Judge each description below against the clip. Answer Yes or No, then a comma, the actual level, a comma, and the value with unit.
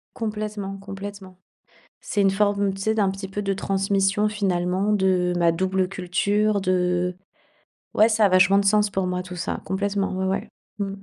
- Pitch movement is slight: Yes, narrow, 1.7 semitones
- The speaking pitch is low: No, high, 195 Hz